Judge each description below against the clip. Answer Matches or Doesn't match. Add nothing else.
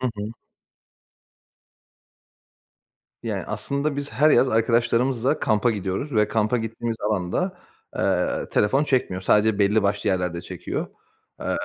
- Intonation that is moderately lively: Matches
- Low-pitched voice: Matches